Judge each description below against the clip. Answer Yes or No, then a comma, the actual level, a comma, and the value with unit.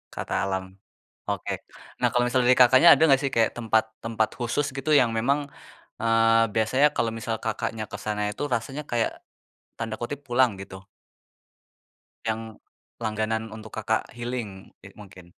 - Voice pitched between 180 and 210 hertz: No, low, 115 Hz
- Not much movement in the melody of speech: Yes, narrow, 1.9 semitones